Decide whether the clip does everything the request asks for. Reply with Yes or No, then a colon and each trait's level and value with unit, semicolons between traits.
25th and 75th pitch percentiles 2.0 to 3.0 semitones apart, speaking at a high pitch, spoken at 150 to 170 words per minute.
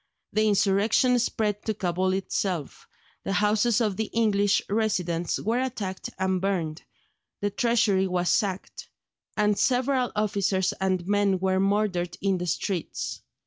No: narrow, 2.4 semitones; high, 200 Hz; slow, 135 wpm